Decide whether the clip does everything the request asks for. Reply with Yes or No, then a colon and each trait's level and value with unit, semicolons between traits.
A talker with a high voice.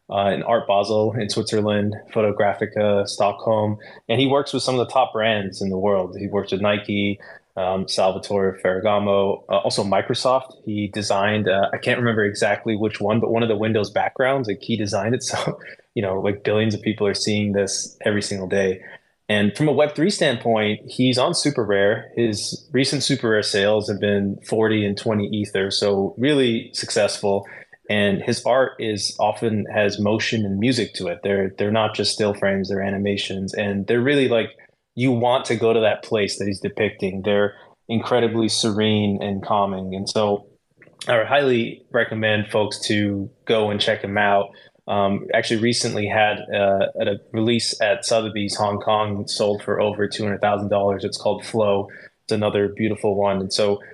No: low, 105 Hz